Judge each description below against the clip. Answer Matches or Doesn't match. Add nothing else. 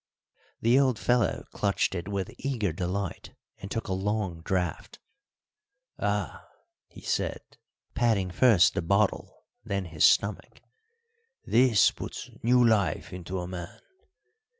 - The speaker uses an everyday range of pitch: Matches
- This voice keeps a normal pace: Doesn't match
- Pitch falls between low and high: Doesn't match